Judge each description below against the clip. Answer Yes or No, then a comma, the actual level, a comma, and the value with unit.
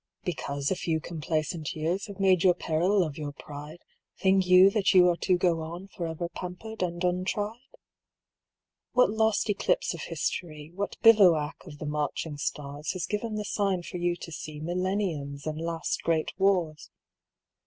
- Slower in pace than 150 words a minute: No, average, 165 wpm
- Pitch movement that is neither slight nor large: Yes, average, 3.7 semitones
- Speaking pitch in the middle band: Yes, medium, 175 Hz